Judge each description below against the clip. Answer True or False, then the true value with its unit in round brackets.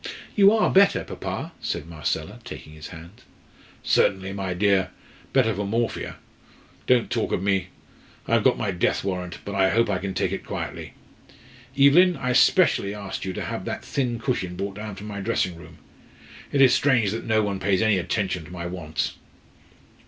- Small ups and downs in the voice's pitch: False (4.0 semitones)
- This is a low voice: True (100 Hz)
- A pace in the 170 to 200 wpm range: True (180 wpm)